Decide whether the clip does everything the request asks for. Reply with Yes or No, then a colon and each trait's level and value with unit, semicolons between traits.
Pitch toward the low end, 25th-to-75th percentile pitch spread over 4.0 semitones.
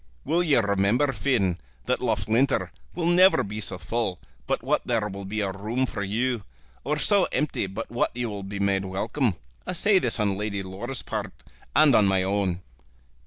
Yes: low, 110 Hz; average, 5.2 semitones